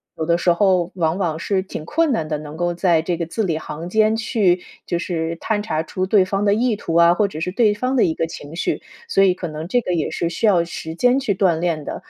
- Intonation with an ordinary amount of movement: Yes, average, 3.9 semitones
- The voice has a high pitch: No, medium, 175 Hz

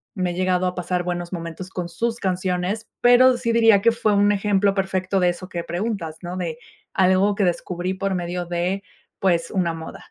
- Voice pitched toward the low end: No, medium, 185 Hz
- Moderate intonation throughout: No, narrow, 2.3 semitones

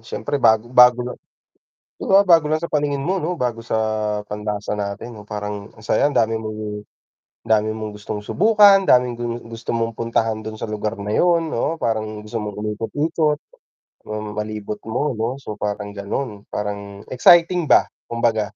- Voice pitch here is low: Yes, low, 110 Hz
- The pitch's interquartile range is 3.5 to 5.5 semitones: Yes, average, 4.9 semitones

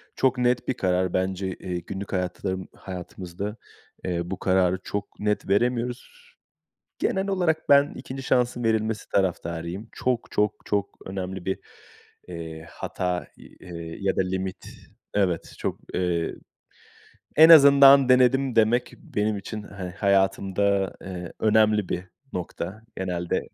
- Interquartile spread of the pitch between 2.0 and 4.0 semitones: No, average, 4.7 semitones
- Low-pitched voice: Yes, low, 100 Hz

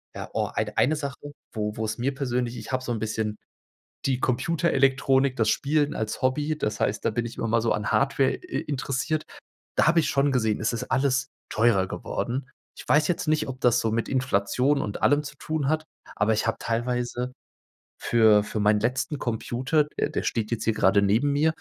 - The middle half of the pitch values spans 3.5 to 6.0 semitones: Yes, average, 4.0 semitones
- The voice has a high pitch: No, low, 125 Hz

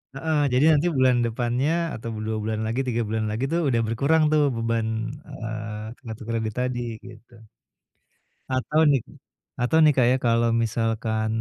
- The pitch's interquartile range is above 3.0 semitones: No, average, 2.7 semitones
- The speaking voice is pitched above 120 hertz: No, low, 115 Hz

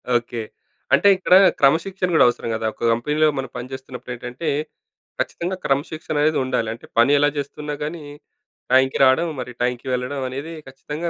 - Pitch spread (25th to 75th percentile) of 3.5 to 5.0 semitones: Yes, average, 3.9 semitones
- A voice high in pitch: No, low, 135 Hz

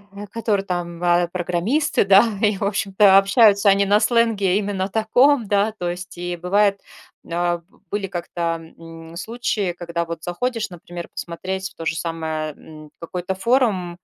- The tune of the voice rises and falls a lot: No, average, 3.1 semitones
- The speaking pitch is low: No, high, 190 Hz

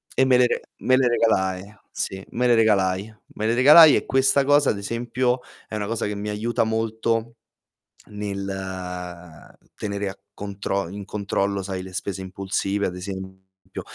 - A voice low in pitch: Yes, low, 100 Hz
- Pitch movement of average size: Yes, average, 3.3 semitones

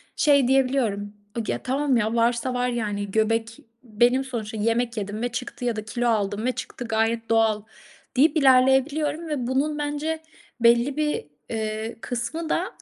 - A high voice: Yes, high, 240 Hz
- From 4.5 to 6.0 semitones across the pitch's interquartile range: No, average, 3.4 semitones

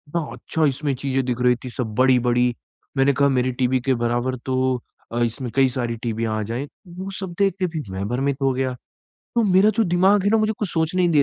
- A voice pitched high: No, low, 135 Hz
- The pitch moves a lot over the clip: Yes, wide, 5.9 semitones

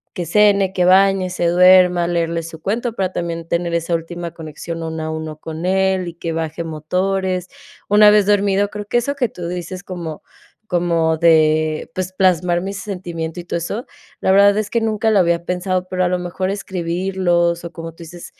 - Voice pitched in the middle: Yes, medium, 180 Hz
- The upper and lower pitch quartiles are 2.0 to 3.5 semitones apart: Yes, narrow, 2.4 semitones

